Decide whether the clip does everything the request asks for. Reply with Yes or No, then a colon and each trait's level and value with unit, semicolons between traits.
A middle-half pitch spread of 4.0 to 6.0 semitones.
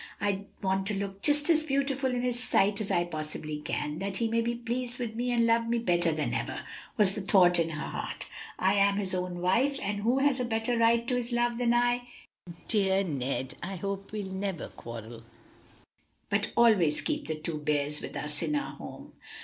Yes: wide, 5.4 semitones